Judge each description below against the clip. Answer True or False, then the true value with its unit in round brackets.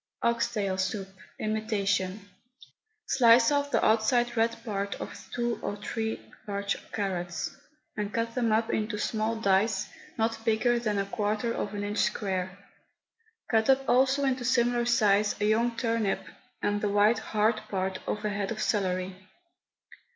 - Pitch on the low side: False (215 Hz)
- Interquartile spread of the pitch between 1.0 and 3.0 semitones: True (2.5 semitones)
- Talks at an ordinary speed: True (150 wpm)